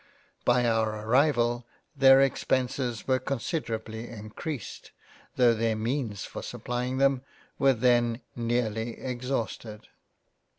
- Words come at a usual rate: No, slow, 110 wpm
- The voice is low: Yes, low, 120 Hz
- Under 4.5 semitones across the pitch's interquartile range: Yes, narrow, 2.6 semitones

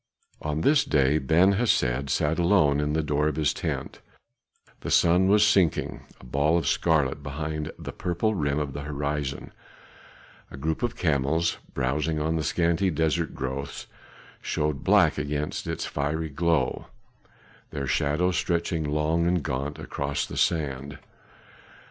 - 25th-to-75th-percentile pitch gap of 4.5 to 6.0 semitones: No, average, 2.8 semitones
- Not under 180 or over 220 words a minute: No, average, 145 wpm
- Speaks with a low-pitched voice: Yes, very low, 75 Hz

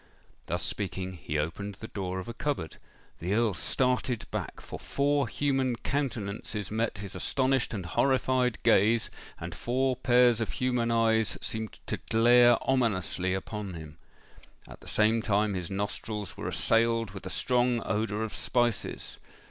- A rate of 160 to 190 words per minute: No, average, 150 wpm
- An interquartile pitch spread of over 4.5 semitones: No, average, 3.7 semitones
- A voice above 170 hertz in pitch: No, low, 110 Hz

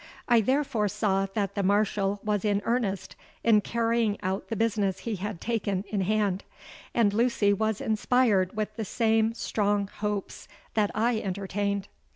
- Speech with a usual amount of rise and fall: No, narrow, 2.0 semitones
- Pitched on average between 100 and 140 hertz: No, high, 210 Hz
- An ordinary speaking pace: Yes, average, 155 wpm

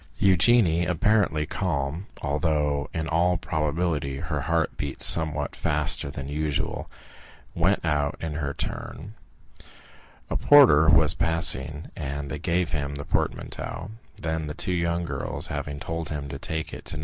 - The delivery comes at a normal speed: Yes, average, 150 wpm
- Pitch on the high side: No, very low, 80 Hz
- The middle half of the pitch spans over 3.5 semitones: No, average, 2.7 semitones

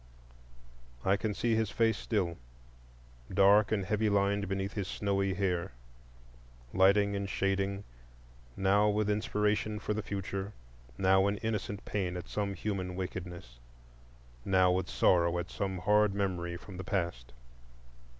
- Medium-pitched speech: No, low, 100 Hz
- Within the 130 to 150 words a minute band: Yes, slow, 135 wpm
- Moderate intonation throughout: No, narrow, 1.9 semitones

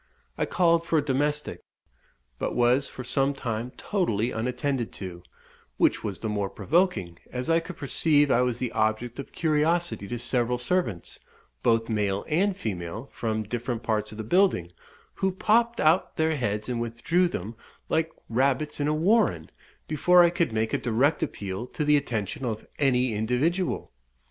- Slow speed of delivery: No, average, 165 wpm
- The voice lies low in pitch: Yes, low, 125 Hz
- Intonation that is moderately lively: No, wide, 6.4 semitones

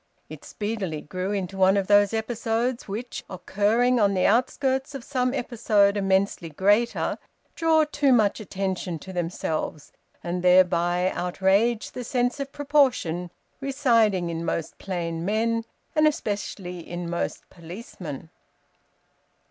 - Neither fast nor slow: No, slow, 125 wpm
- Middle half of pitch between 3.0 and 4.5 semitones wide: No, average, 5.0 semitones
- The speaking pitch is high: Yes, high, 200 Hz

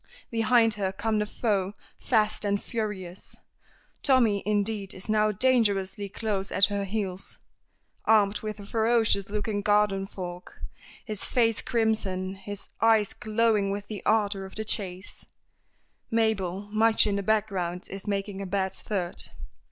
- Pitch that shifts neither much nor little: No, narrow, 2.1 semitones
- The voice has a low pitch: No, high, 205 Hz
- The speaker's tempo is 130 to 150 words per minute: Yes, average, 140 wpm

